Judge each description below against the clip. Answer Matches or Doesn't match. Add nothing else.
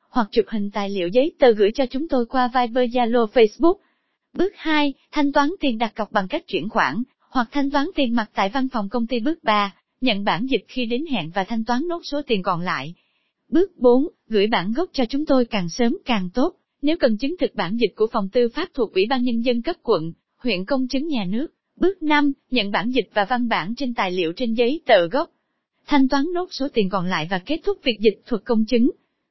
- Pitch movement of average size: Matches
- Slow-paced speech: Doesn't match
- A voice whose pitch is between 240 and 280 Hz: Matches